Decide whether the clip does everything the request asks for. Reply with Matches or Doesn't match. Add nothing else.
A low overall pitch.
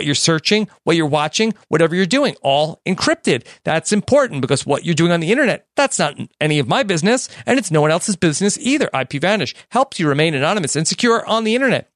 Doesn't match